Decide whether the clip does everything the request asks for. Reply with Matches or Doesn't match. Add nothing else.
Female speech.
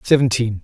Doesn't match